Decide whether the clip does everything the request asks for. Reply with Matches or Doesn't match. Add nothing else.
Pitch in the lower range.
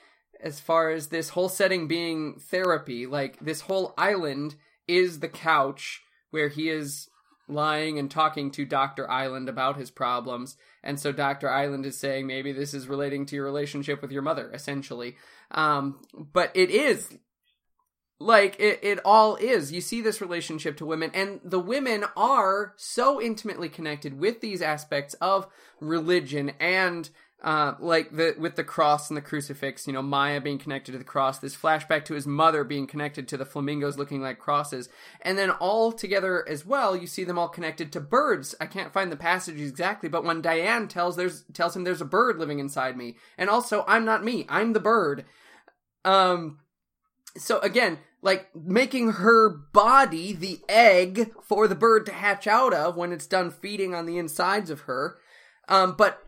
Doesn't match